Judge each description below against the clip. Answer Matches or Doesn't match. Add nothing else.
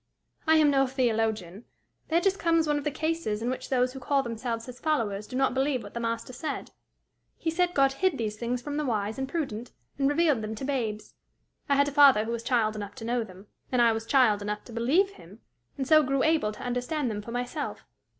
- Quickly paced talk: Matches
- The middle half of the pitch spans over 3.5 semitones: Matches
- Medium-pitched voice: Doesn't match